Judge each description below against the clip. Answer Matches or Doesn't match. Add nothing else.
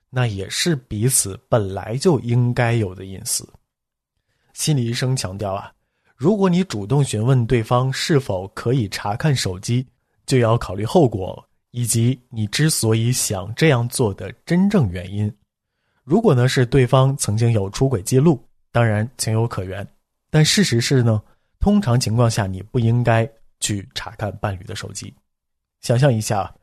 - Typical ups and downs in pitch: Matches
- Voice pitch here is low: Matches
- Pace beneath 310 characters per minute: Matches